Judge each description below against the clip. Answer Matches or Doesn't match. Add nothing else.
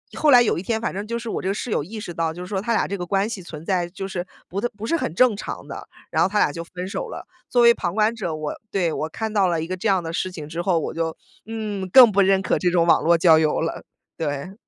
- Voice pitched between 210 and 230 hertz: Doesn't match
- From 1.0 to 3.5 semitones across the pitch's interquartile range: Doesn't match